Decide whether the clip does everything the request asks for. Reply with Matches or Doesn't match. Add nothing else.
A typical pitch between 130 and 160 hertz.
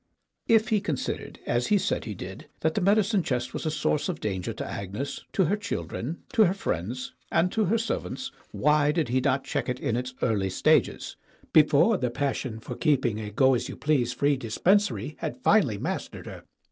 Matches